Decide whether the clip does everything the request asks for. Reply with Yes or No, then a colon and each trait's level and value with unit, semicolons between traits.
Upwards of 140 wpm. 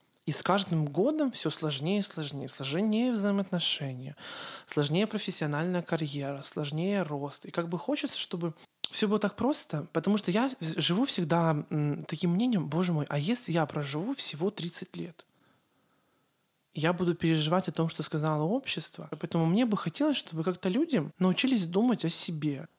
Yes: average, 155 wpm